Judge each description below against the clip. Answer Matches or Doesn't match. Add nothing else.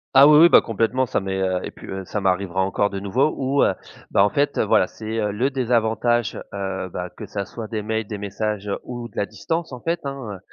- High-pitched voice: Doesn't match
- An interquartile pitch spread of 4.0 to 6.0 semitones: Matches